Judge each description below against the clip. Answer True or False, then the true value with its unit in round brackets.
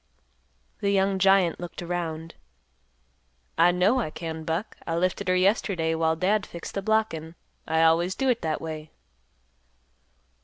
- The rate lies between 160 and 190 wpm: False (145 wpm)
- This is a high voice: False (175 Hz)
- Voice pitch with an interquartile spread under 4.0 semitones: True (3.2 semitones)